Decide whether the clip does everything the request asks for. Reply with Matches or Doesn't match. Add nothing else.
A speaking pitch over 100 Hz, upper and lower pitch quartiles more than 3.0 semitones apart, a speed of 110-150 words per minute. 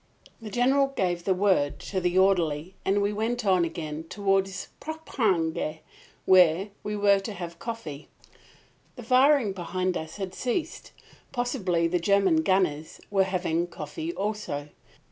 Matches